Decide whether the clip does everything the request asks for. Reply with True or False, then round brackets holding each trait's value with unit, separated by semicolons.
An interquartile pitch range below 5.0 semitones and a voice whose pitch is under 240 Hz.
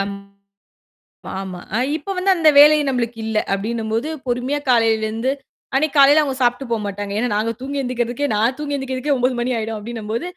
False (3.9 semitones; 245 Hz)